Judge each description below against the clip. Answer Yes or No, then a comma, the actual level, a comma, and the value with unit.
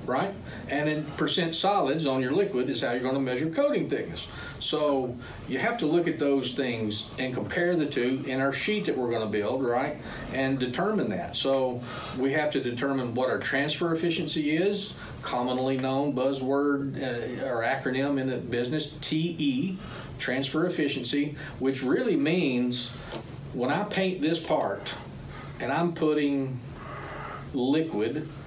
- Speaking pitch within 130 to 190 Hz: Yes, medium, 140 Hz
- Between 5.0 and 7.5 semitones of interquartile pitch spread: No, average, 3.1 semitones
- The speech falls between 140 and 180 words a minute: Yes, average, 155 wpm